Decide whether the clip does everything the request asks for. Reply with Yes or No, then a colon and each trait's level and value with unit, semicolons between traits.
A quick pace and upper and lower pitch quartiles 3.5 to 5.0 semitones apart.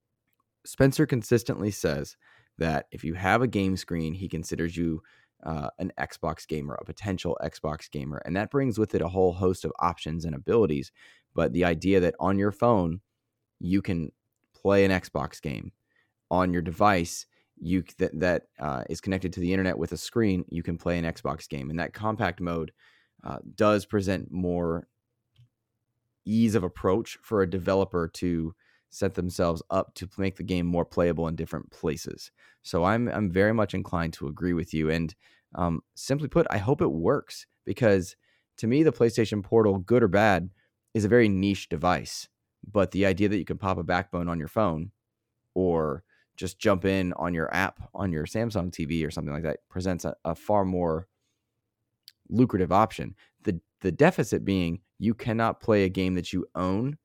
No: average, 180 wpm; average, 4.0 semitones